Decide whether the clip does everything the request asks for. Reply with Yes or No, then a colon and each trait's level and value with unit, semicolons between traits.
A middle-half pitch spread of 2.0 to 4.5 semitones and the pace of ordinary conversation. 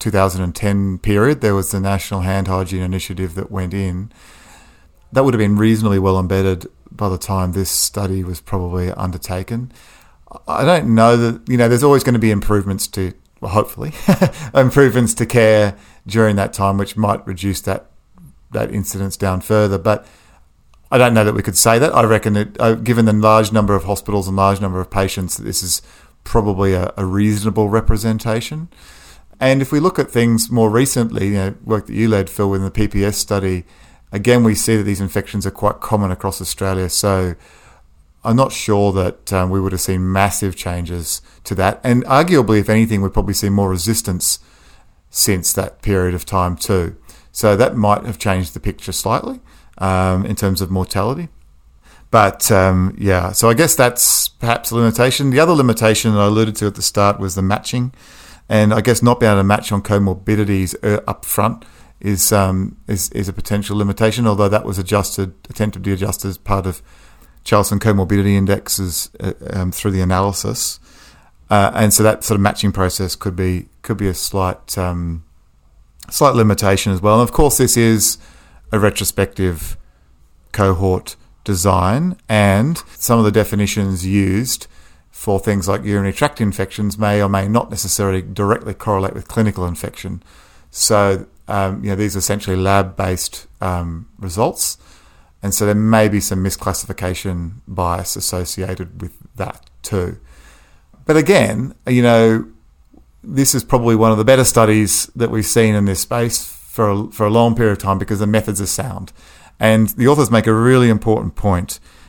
Yes: average, 2.9 semitones; average, 175 wpm